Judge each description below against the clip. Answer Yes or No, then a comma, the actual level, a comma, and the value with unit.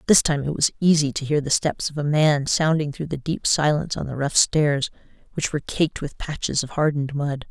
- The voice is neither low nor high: Yes, medium, 150 Hz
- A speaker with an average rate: No, fast, 230 wpm